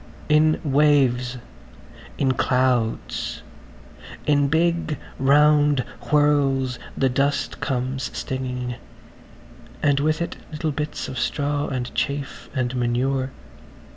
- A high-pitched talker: No, medium, 140 Hz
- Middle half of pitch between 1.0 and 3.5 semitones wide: Yes, narrow, 2.5 semitones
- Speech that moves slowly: Yes, slow, 100 wpm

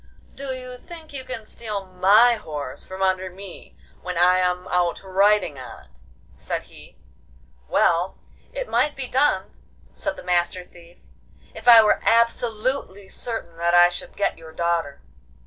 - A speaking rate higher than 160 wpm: No, average, 155 wpm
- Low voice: No, high, 190 Hz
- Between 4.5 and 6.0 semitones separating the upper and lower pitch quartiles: Yes, average, 4.9 semitones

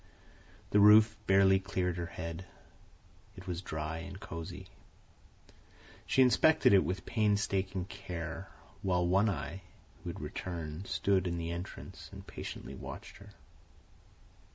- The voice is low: Yes, very low, 95 Hz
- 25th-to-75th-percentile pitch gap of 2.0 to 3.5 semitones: Yes, narrow, 2.4 semitones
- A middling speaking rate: No, slow, 130 wpm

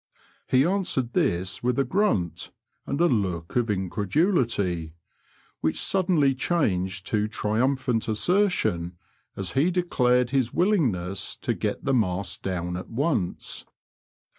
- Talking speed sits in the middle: No, slow, 120 wpm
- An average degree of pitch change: No, wide, 7.4 semitones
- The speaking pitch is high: No, low, 115 Hz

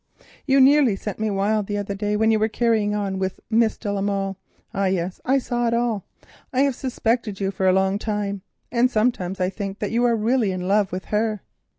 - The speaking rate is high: Yes, fast, 215 wpm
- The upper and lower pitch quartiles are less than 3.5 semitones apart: Yes, average, 3.0 semitones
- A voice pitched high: Yes, high, 210 Hz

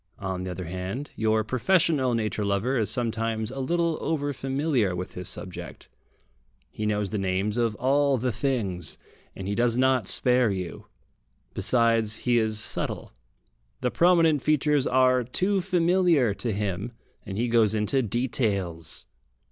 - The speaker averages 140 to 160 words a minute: Yes, average, 150 wpm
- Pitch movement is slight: No, average, 4.7 semitones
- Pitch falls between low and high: No, low, 115 Hz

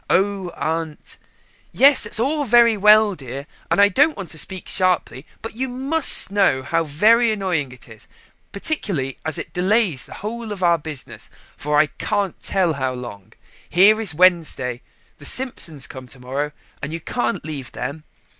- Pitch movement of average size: No, wide, 7.0 semitones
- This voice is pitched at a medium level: Yes, medium, 180 Hz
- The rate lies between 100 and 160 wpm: No, average, 175 wpm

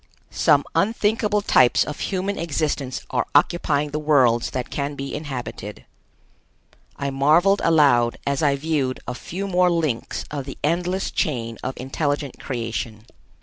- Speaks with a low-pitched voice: No, medium, 145 Hz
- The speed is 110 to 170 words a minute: Yes, average, 140 wpm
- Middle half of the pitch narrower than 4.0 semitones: No, average, 4.5 semitones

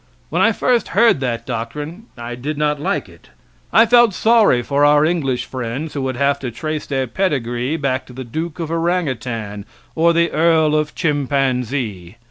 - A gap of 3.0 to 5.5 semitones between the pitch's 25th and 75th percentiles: Yes, average, 4.7 semitones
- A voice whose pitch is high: No, medium, 145 Hz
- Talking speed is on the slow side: No, average, 175 wpm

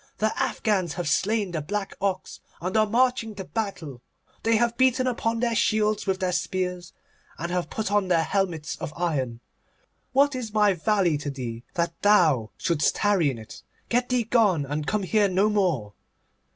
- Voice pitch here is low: No, high, 195 Hz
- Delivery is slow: No, average, 180 wpm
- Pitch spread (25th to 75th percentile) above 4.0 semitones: Yes, average, 4.7 semitones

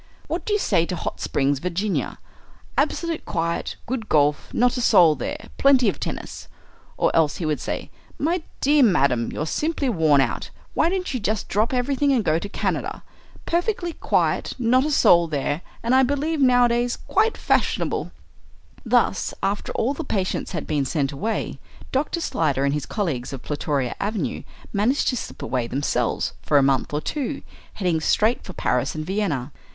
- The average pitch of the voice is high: Yes, high, 205 Hz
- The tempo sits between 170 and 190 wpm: Yes, average, 175 wpm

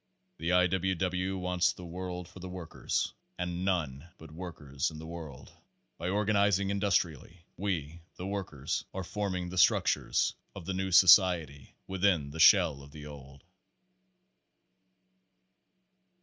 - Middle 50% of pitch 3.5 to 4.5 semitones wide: No, average, 3.1 semitones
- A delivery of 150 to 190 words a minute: No, average, 140 wpm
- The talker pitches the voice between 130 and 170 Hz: No, very low, 90 Hz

